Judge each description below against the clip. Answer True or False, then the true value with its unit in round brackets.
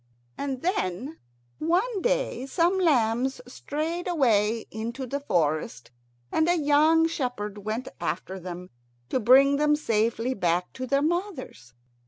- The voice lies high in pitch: True (260 Hz)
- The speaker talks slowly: True (130 wpm)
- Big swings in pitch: True (6.9 semitones)